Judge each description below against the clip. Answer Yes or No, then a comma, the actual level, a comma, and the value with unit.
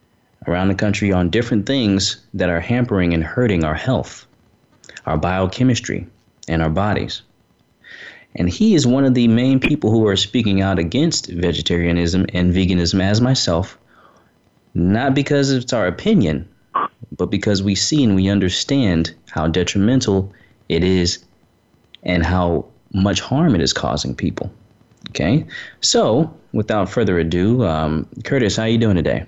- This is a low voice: Yes, very low, 95 Hz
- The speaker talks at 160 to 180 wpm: No, average, 150 wpm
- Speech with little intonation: No, average, 4.9 semitones